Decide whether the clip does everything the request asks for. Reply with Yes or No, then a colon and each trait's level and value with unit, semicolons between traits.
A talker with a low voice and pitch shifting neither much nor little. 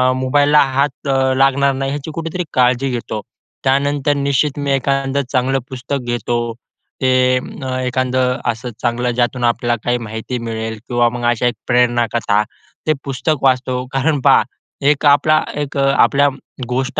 No: low, 130 Hz; narrow, 2.3 semitones